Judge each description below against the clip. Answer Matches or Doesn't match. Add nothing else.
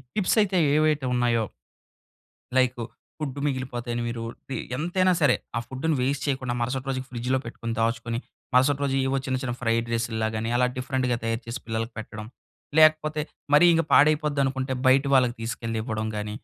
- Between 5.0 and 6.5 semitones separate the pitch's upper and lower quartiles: Doesn't match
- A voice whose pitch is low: Matches